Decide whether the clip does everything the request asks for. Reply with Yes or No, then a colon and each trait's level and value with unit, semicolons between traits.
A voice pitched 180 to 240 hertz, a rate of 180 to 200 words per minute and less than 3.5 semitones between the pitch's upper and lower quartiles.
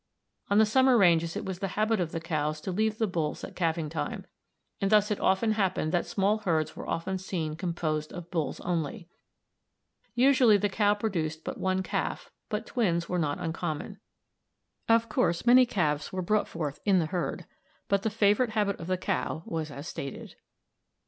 No: medium, 185 Hz; average, 185 wpm; average, 4.4 semitones